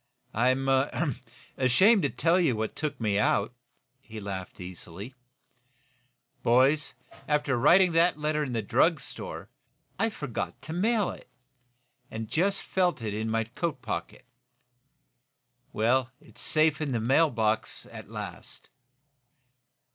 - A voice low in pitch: Yes, low, 130 Hz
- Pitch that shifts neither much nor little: No, wide, 6.4 semitones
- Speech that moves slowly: Yes, slow, 130 wpm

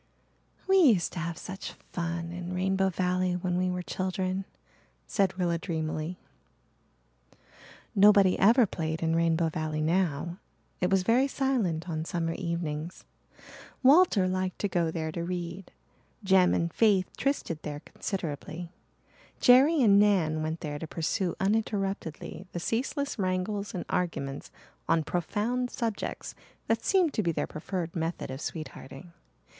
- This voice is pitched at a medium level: Yes, medium, 180 Hz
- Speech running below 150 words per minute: Yes, average, 140 wpm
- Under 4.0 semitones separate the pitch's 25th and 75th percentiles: Yes, average, 3.3 semitones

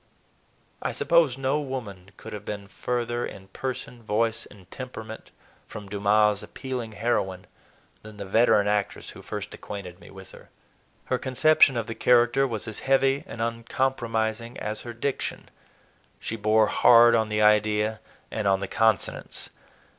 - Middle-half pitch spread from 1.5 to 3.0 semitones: Yes, average, 2.7 semitones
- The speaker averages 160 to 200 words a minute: No, average, 150 wpm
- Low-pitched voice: Yes, low, 110 Hz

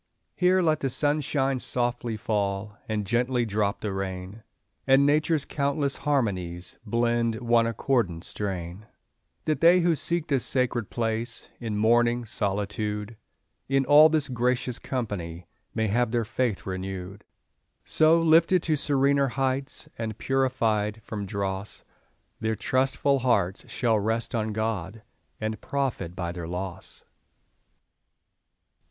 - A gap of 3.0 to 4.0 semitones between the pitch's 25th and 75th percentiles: No, average, 4.7 semitones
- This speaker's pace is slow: Yes, slow, 125 wpm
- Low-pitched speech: Yes, low, 115 Hz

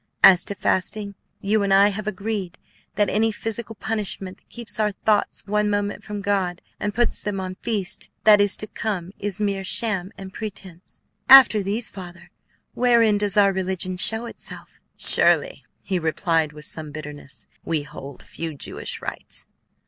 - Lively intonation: No, average, 2.7 semitones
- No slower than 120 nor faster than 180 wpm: Yes, average, 165 wpm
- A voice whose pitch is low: No, high, 200 Hz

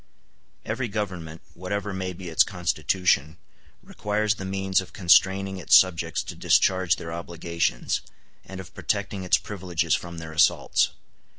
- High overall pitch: No, very low, 95 Hz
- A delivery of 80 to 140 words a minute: Yes, slow, 135 wpm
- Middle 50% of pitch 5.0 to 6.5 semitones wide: No, narrow, 2.5 semitones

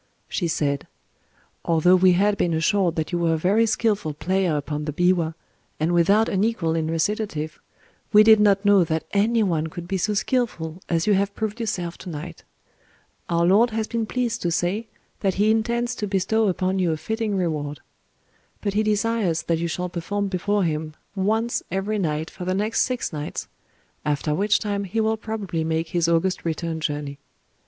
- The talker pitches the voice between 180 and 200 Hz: Yes, medium, 185 Hz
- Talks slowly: No, average, 185 wpm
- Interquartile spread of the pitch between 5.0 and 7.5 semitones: No, average, 4.4 semitones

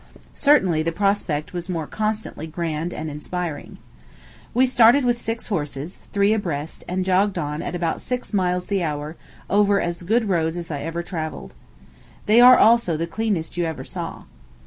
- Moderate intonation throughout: Yes, average, 4.5 semitones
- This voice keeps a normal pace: Yes, average, 170 wpm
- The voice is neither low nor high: Yes, medium, 175 Hz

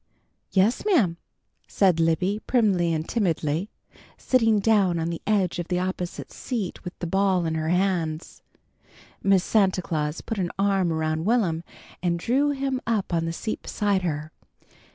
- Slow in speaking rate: No, average, 155 wpm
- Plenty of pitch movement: No, average, 4.0 semitones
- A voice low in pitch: No, medium, 185 Hz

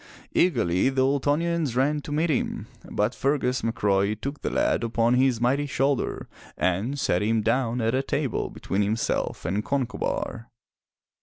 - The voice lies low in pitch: Yes, low, 125 Hz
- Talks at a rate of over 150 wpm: No, average, 145 wpm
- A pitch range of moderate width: Yes, average, 3.9 semitones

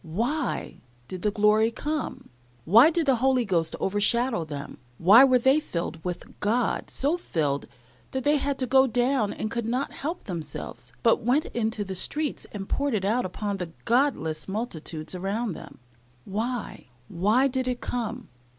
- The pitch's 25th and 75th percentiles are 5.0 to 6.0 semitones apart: Yes, wide, 5.4 semitones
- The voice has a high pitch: Yes, high, 230 Hz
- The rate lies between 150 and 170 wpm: Yes, average, 165 wpm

